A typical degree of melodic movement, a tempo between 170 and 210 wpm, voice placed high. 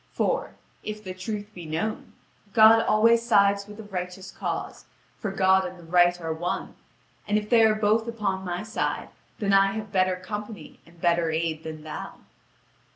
Yes: average, 3.4 semitones; average, 175 wpm; high, 195 Hz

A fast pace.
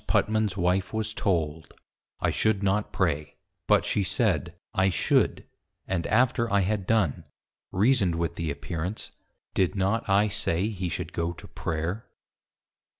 No: average, 145 wpm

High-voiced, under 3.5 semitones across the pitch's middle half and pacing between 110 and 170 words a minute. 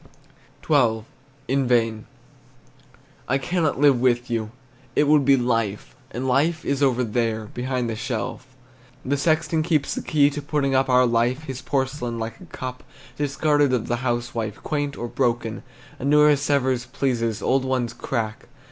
No: low, 130 Hz; average, 3.1 semitones; average, 155 wpm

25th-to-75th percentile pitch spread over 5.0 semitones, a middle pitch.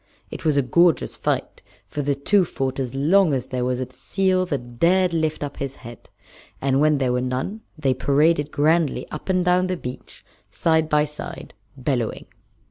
No: average, 4.4 semitones; medium, 145 Hz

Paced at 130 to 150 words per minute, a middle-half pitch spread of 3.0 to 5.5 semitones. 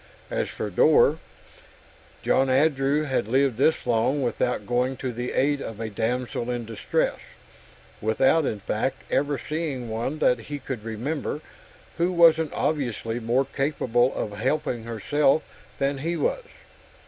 Yes: average, 140 wpm; average, 3.8 semitones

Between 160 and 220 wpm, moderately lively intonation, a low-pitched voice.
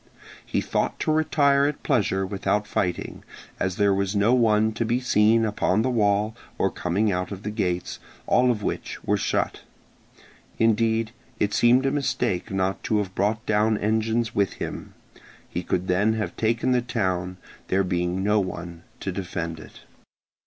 Yes: average, 165 wpm; average, 3.3 semitones; low, 105 Hz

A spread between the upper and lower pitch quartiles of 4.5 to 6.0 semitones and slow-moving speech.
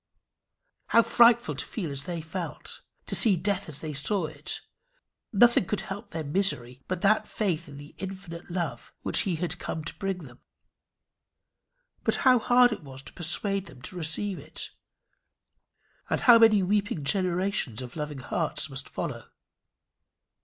No: average, 5.0 semitones; average, 160 wpm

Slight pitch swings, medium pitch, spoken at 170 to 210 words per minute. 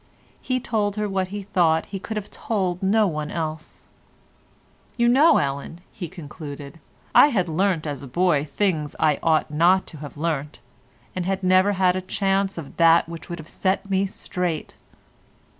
No: average, 3.9 semitones; medium, 180 Hz; average, 180 wpm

